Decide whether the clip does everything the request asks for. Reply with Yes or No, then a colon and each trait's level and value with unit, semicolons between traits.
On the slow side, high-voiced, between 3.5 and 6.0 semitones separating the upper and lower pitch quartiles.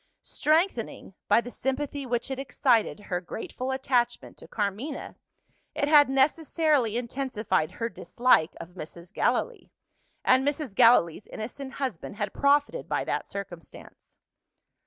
Yes: slow, 125 wpm; very high, 250 Hz; average, 5.2 semitones